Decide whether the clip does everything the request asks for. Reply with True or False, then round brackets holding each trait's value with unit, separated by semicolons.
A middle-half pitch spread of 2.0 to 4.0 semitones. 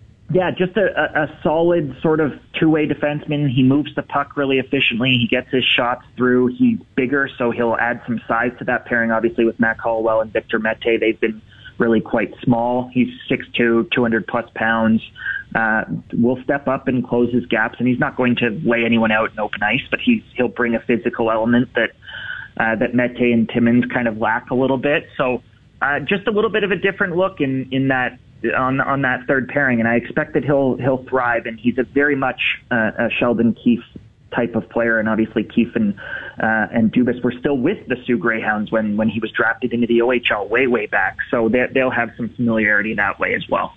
True (3.1 semitones)